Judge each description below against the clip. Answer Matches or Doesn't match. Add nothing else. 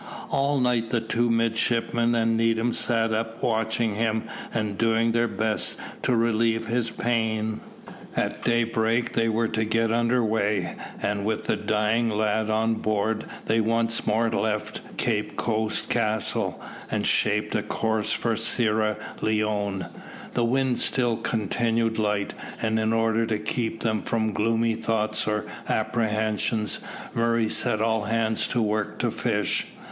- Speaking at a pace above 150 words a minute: Doesn't match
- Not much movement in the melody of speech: Matches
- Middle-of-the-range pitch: Doesn't match